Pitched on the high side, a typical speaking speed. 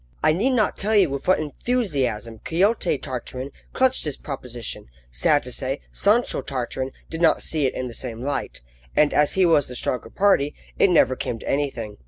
No: medium, 145 Hz; average, 190 wpm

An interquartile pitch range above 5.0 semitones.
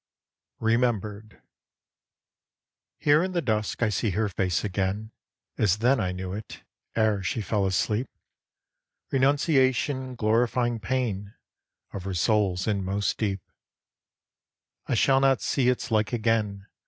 No: average, 3.9 semitones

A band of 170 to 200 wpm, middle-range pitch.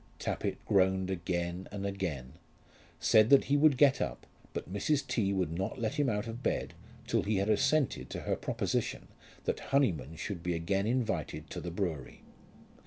No: average, 175 wpm; low, 100 Hz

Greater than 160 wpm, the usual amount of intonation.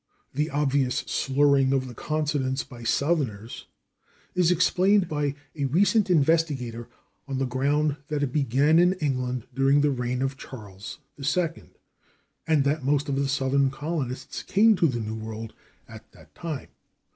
No: average, 150 wpm; average, 3.1 semitones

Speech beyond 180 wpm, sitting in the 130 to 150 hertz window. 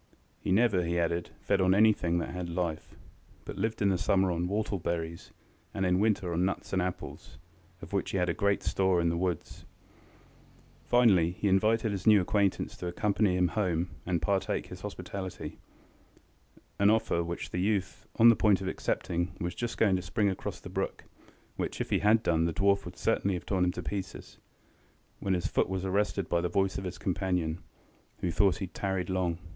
No: average, 200 wpm; very low, 95 Hz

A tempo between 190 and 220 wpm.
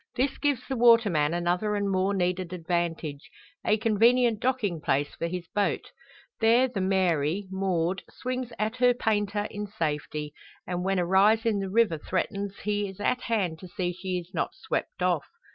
No: average, 175 wpm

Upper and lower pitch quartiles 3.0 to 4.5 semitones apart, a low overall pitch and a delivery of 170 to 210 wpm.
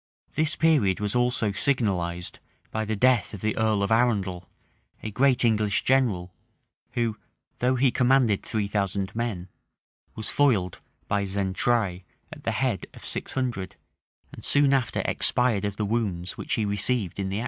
No: average, 3.9 semitones; low, 110 Hz; average, 160 wpm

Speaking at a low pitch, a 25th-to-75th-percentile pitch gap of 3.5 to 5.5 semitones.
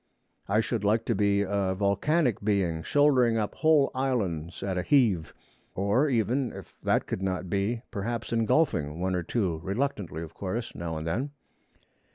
Yes: low, 100 Hz; average, 4.5 semitones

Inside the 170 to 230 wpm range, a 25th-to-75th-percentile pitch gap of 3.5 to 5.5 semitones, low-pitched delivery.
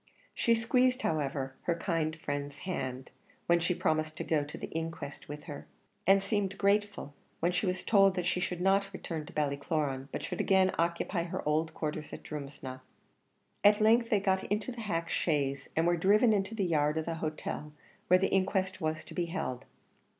No: average, 190 wpm; average, 4.4 semitones; medium, 170 Hz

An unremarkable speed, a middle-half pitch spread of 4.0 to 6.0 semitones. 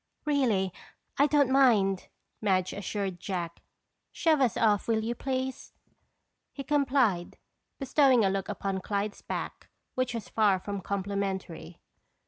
No: slow, 125 wpm; average, 5.3 semitones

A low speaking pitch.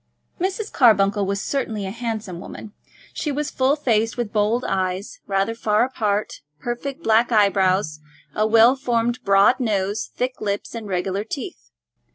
No: high, 220 Hz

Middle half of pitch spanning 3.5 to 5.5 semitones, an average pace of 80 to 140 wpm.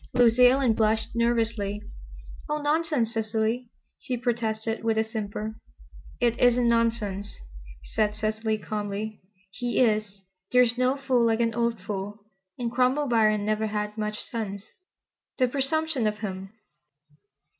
No: narrow, 2.4 semitones; slow, 135 wpm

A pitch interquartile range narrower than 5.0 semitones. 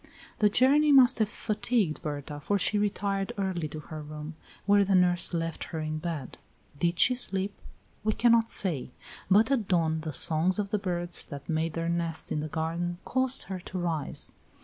Yes: average, 4.5 semitones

